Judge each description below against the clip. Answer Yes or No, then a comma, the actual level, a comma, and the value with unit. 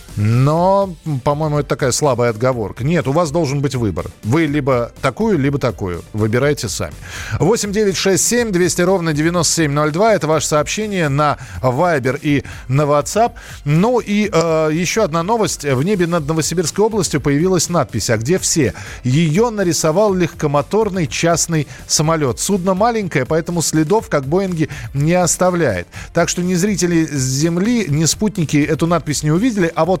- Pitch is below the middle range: No, medium, 160 Hz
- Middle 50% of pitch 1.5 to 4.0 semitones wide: No, average, 4.4 semitones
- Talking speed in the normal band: Yes, average, 145 wpm